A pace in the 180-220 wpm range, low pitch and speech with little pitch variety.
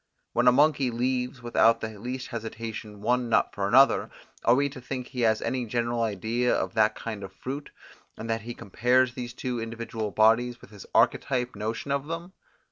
Yes: average, 190 wpm; low, 120 Hz; narrow, 2.3 semitones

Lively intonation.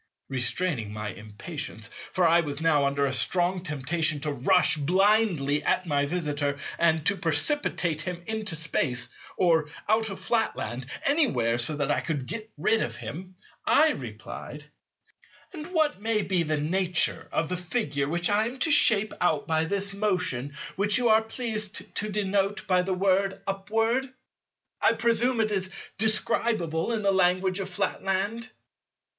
Yes: wide, 6.2 semitones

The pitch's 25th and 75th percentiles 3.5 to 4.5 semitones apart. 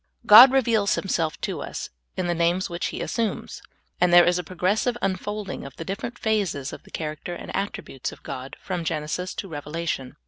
Yes: average, 4.2 semitones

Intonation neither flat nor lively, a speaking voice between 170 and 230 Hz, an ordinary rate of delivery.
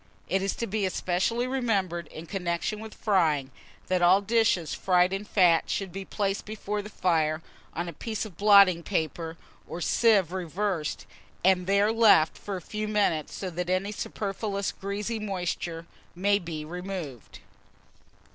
Yes: average, 3.2 semitones; high, 190 Hz; average, 155 wpm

